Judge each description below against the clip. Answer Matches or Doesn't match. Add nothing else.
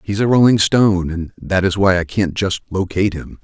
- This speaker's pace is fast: Matches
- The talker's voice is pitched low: Matches